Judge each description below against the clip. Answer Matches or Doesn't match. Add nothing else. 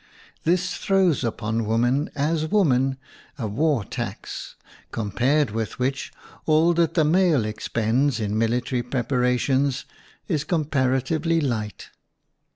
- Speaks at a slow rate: Matches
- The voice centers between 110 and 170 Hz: Matches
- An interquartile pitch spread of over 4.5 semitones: Matches